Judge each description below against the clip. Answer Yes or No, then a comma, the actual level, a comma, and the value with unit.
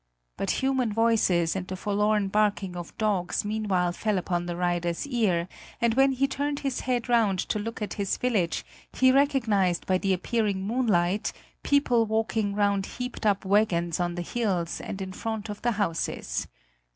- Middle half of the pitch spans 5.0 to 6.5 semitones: No, average, 4.2 semitones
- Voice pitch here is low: No, high, 205 Hz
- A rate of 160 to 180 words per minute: Yes, average, 170 wpm